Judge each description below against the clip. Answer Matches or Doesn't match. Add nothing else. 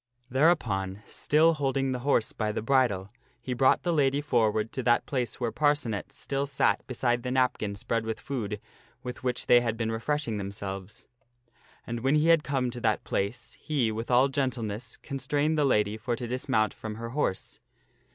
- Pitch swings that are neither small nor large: Matches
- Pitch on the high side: Doesn't match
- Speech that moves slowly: Doesn't match